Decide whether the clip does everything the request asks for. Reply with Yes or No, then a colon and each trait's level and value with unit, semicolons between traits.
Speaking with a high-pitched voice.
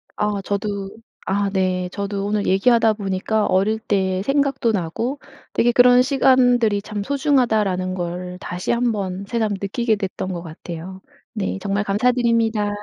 Yes: high, 205 Hz